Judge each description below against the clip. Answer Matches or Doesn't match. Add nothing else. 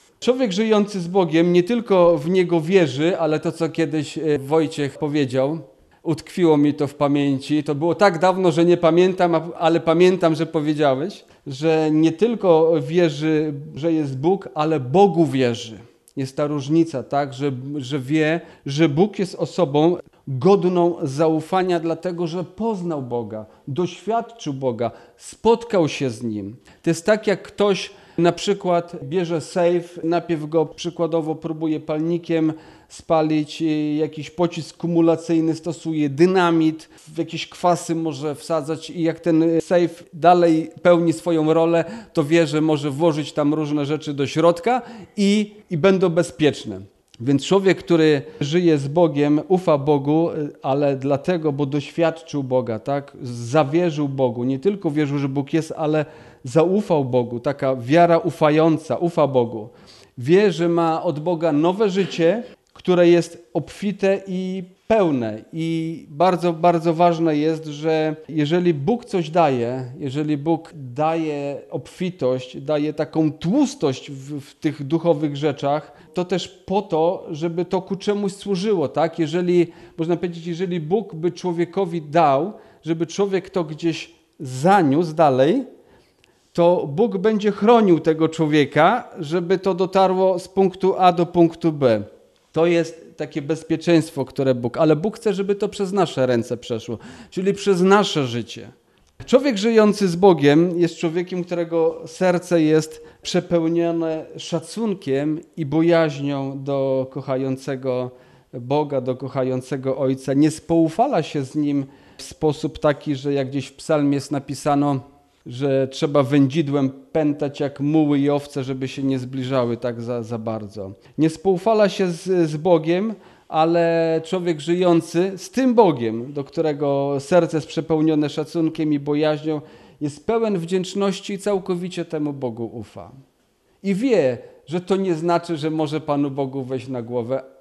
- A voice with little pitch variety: Doesn't match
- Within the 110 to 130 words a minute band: Doesn't match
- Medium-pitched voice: Matches